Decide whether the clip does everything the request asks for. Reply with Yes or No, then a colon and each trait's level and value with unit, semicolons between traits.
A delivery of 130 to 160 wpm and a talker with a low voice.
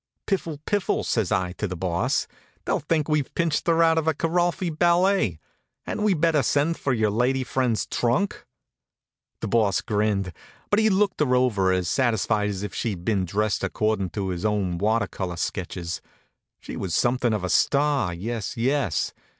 No: average, 175 wpm; low, 115 Hz